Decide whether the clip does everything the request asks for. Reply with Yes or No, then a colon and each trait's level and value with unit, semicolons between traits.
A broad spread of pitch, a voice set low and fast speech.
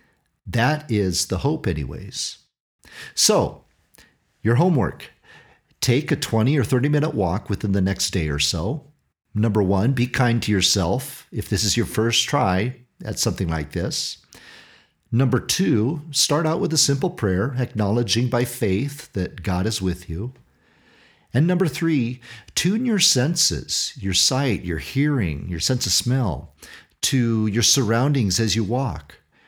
No: wide, 5.8 semitones; low, 115 Hz; average, 150 wpm